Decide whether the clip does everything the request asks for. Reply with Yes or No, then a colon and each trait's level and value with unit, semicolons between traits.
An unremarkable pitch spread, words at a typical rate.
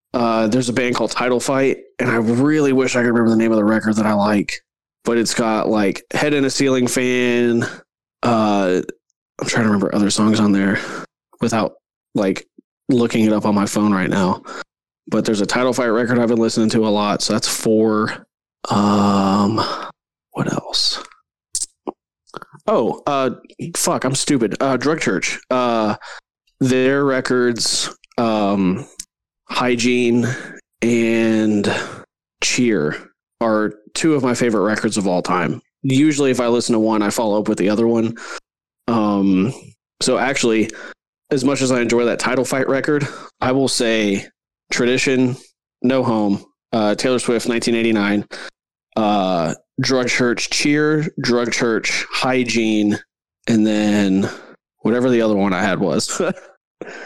Yes: average, 3.0 semitones; average, 150 wpm